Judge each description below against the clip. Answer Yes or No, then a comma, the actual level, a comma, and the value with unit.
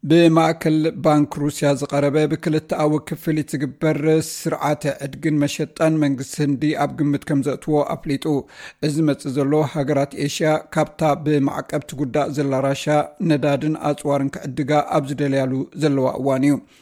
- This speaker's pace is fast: Yes, fast, 120 wpm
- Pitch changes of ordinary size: No, narrow, 1.6 semitones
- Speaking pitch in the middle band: Yes, medium, 150 Hz